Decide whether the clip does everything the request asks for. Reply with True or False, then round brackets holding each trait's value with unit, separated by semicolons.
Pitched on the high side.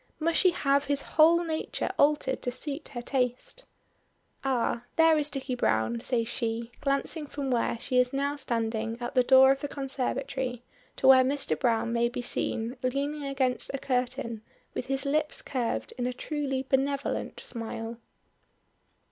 True (265 Hz)